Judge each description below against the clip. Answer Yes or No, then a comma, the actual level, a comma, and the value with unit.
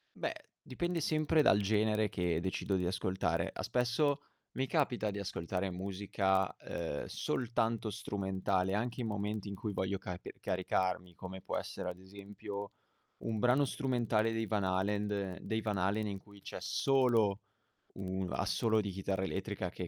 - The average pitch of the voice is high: No, low, 100 Hz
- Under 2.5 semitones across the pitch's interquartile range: No, average, 2.9 semitones